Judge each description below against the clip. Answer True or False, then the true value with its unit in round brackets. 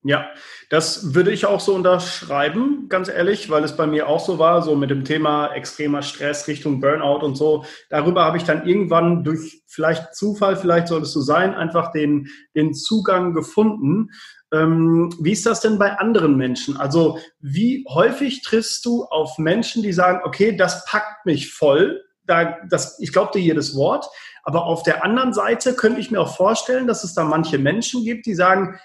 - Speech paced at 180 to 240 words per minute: True (190 wpm)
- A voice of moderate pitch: True (170 Hz)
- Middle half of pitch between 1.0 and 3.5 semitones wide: False (5.0 semitones)